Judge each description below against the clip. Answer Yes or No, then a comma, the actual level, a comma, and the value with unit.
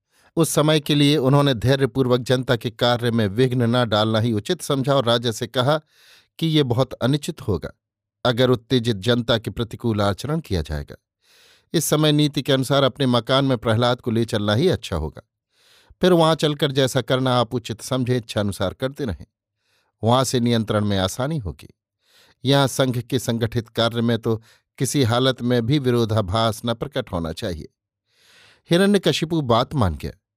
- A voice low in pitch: Yes, low, 125 Hz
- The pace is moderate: Yes, average, 170 wpm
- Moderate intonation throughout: Yes, average, 3.5 semitones